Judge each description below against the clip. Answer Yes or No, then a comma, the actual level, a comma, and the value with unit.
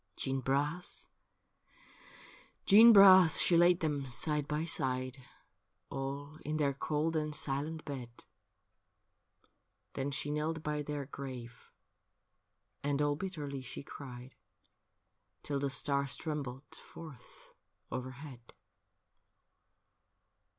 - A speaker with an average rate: No, slow, 100 wpm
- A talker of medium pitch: Yes, medium, 145 Hz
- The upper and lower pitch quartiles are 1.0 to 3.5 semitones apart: Yes, narrow, 2.4 semitones